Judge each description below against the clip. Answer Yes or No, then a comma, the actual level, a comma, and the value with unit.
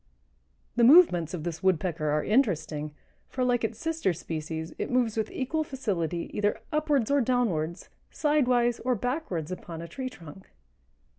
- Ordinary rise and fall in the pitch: No, wide, 7.5 semitones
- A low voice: No, high, 210 Hz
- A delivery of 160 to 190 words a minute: No, average, 150 wpm